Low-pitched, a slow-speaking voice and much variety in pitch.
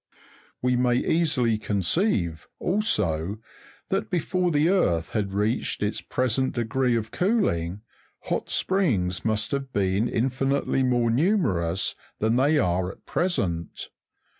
Yes: low, 115 Hz; slow, 125 wpm; wide, 7.1 semitones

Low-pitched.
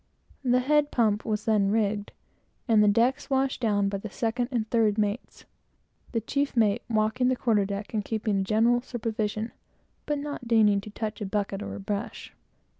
No: high, 220 Hz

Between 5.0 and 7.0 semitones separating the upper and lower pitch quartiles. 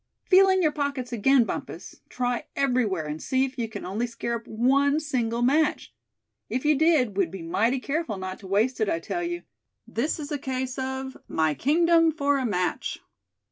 No: average, 4.6 semitones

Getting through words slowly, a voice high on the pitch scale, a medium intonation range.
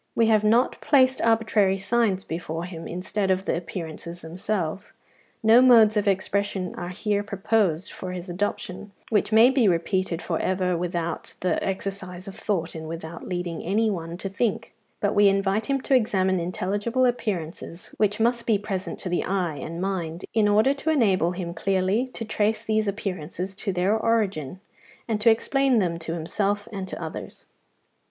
No: average, 170 wpm; high, 195 Hz; average, 3.5 semitones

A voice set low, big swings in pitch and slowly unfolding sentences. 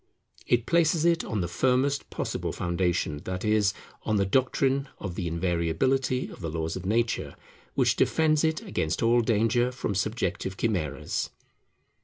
No: low, 110 Hz; wide, 6.5 semitones; average, 150 wpm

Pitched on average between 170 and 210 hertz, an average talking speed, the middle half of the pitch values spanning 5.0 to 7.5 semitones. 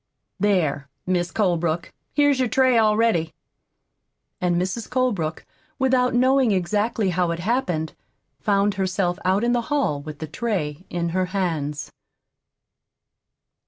No: high, 190 Hz; slow, 125 wpm; wide, 5.6 semitones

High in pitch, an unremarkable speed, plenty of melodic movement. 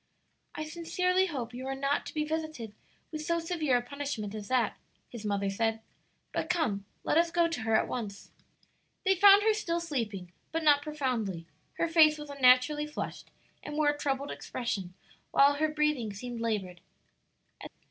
Yes: very high, 285 Hz; average, 170 wpm; wide, 5.8 semitones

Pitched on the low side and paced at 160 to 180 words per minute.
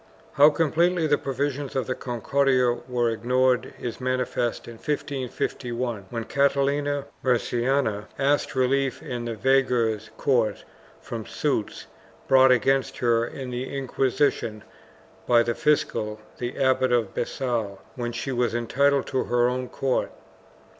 No: low, 125 Hz; slow, 135 wpm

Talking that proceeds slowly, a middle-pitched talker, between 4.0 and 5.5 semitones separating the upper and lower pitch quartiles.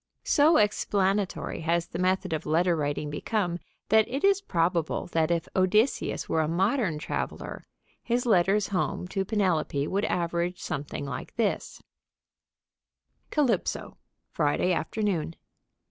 Yes: slow, 125 wpm; medium, 180 Hz; average, 4.3 semitones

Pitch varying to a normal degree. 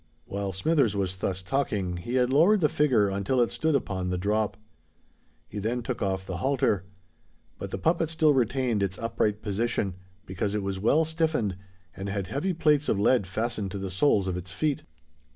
No: wide, 6.0 semitones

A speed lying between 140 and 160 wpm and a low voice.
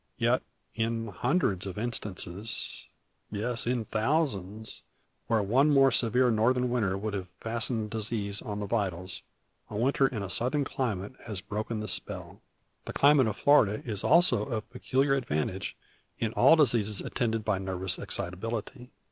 Yes: average, 150 wpm; low, 110 Hz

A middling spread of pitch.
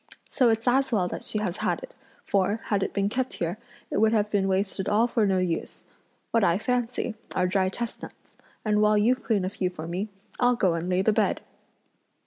Yes: average, 3.3 semitones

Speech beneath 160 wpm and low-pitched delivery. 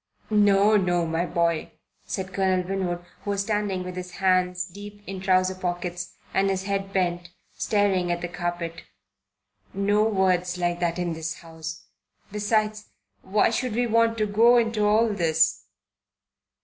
No: average, 150 wpm; medium, 185 Hz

